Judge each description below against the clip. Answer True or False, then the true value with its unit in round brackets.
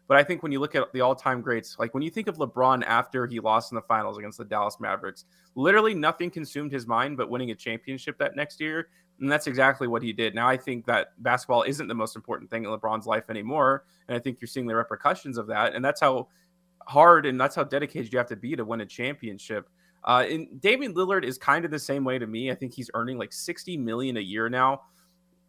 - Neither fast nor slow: False (245 wpm)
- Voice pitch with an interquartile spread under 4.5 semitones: False (4.9 semitones)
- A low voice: True (130 Hz)